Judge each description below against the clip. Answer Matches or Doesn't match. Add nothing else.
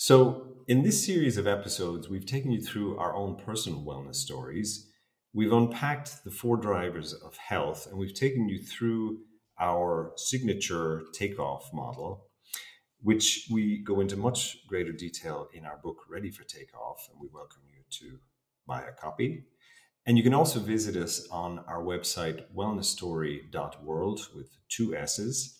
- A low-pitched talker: Matches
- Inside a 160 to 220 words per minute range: Doesn't match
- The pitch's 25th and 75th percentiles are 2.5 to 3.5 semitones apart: Doesn't match